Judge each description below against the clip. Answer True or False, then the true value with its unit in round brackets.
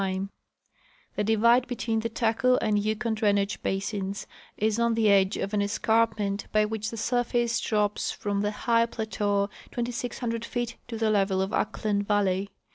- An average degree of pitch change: False (2.2 semitones)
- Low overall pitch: False (215 Hz)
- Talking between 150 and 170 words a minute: True (155 wpm)